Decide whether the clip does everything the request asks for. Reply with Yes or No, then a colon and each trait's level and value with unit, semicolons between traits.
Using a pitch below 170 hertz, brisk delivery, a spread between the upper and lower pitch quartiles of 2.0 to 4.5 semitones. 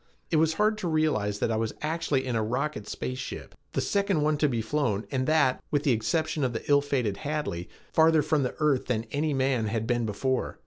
No: low, 135 Hz; fast, 225 wpm; average, 5.0 semitones